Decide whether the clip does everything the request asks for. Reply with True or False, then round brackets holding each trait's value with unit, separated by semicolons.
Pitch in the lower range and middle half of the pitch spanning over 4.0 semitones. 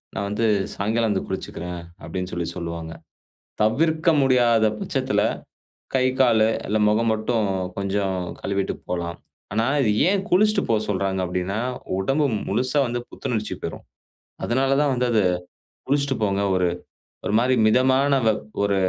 True (110 Hz; 4.9 semitones)